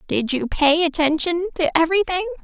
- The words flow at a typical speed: Yes, average, 150 wpm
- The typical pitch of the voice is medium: No, very high, 330 Hz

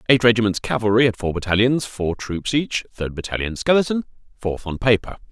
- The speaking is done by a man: Yes, male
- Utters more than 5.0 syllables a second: Yes, 5.6 syllables/s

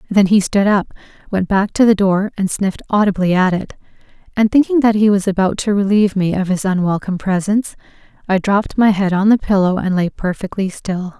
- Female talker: Yes, female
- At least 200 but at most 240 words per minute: Yes, fast, 205 wpm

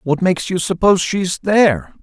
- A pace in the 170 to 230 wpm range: Yes, fast, 205 wpm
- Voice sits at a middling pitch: Yes, medium, 180 Hz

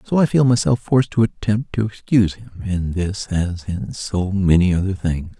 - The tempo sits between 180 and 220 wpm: Yes, average, 200 wpm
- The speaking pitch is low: Yes, low, 100 Hz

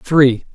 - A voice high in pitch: No, low, 135 Hz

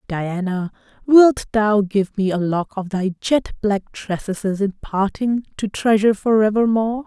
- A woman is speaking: Yes, female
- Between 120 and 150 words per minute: Yes, average, 145 wpm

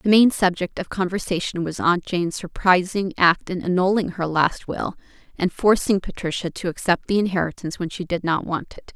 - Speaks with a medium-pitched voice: Yes, medium, 180 Hz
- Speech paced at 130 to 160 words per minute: No, average, 190 wpm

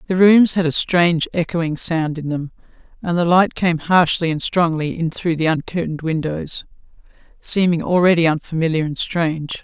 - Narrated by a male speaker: No, female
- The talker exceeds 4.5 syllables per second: Yes, 5.0 syllables/s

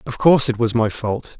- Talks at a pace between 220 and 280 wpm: Yes, fast, 260 wpm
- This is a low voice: Yes, low, 120 Hz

